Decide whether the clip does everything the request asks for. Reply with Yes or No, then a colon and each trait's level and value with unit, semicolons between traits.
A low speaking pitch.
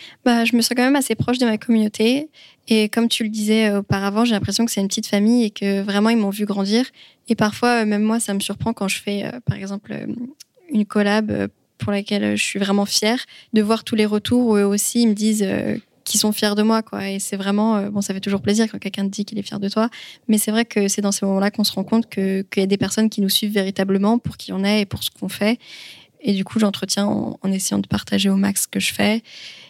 No: high, 210 Hz